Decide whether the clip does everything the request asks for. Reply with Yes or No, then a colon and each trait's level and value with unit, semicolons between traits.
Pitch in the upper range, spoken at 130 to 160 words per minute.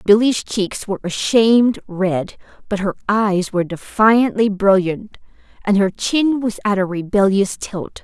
Yes: high, 205 Hz; average, 150 wpm